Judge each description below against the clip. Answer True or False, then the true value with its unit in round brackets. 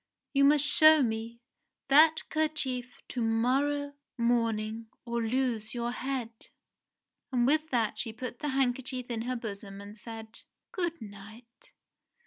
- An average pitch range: True (3.4 semitones)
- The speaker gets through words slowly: True (130 wpm)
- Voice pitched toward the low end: False (245 Hz)